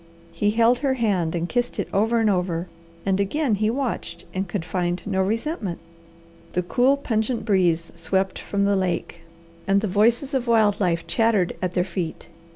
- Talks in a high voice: Yes, high, 200 Hz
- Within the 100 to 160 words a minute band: No, average, 175 wpm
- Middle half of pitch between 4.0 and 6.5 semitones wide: Yes, average, 4.3 semitones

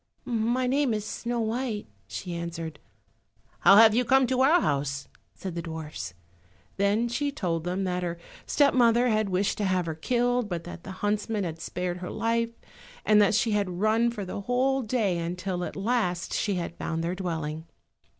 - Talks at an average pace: Yes, average, 185 wpm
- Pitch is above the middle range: Yes, high, 200 Hz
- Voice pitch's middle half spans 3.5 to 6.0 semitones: Yes, average, 5.2 semitones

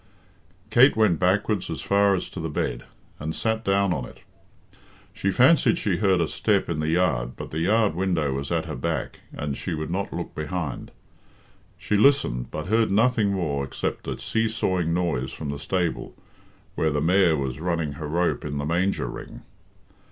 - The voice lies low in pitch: Yes, very low, 85 Hz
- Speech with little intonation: No, average, 4.7 semitones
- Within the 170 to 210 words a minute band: Yes, average, 185 wpm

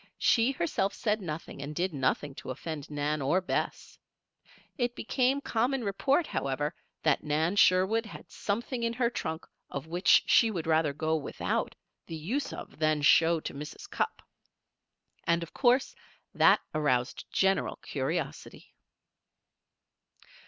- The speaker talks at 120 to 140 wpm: Yes, slow, 135 wpm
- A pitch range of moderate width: No, wide, 7.0 semitones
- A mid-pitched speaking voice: Yes, medium, 170 Hz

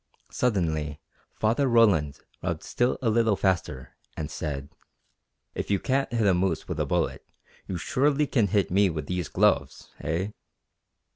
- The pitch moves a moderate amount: No, wide, 6.5 semitones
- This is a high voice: No, very low, 95 Hz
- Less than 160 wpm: Yes, average, 150 wpm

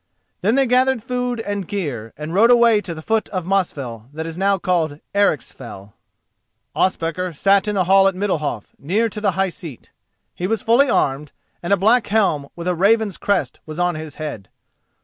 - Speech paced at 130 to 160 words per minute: No, average, 190 wpm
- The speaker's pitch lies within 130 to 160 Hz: No, high, 190 Hz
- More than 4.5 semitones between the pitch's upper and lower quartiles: Yes, average, 5.0 semitones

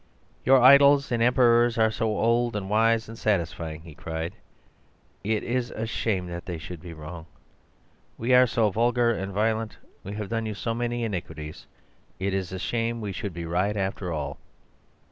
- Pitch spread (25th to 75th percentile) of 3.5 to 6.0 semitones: Yes, average, 4.7 semitones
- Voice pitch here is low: Yes, low, 110 Hz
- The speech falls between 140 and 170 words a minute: No, average, 180 wpm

